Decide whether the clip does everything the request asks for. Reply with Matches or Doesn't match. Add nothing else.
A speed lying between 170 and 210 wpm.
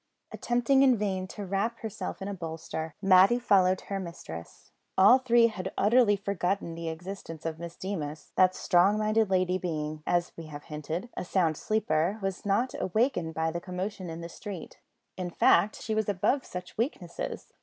Matches